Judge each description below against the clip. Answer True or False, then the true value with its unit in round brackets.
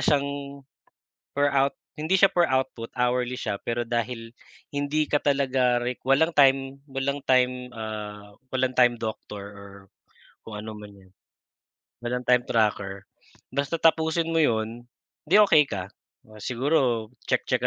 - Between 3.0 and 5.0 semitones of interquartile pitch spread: True (3.7 semitones)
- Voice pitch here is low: True (125 Hz)